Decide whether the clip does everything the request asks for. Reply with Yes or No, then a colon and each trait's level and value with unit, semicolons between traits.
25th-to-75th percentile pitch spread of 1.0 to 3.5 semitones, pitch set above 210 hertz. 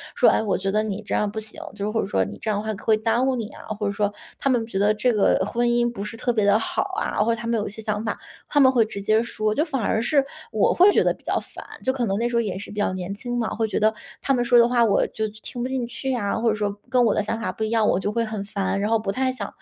Yes: narrow, 2.5 semitones; high, 220 Hz